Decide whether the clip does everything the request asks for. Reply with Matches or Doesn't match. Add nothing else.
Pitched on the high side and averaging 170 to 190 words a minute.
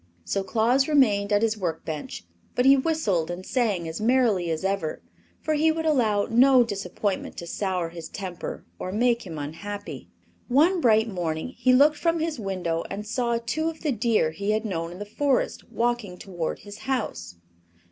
Matches